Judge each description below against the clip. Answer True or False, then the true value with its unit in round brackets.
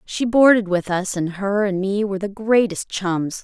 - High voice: True (200 Hz)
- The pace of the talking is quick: True (210 wpm)